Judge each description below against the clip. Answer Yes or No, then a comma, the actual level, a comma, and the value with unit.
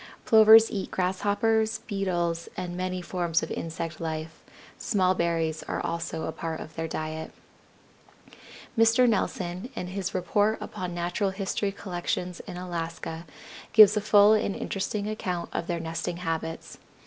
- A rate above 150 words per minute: No, average, 140 wpm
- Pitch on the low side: No, medium, 180 Hz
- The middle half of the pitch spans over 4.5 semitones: No, average, 3.5 semitones